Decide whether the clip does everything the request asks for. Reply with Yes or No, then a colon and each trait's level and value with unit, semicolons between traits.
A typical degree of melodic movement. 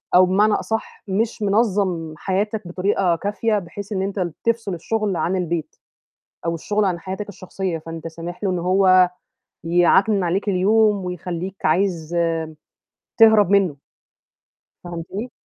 Yes: average, 3.0 semitones